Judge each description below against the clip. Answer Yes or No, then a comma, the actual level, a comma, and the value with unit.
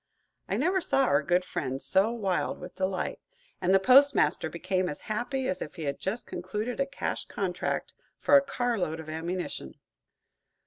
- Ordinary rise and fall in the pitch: No, wide, 6.0 semitones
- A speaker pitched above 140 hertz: Yes, high, 190 Hz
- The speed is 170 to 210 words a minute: Yes, average, 175 wpm